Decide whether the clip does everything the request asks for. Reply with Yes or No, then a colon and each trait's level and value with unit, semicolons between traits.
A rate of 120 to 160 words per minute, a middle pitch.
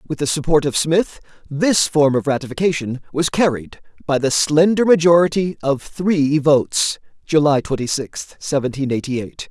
Yes: average, 150 wpm; medium, 150 Hz